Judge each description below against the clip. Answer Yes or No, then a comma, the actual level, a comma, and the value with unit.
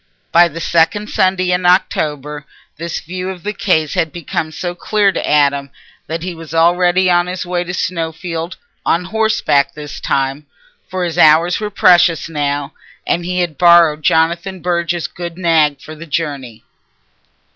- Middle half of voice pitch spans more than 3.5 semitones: No, average, 2.7 semitones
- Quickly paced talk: No, average, 160 wpm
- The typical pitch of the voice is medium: Yes, medium, 170 Hz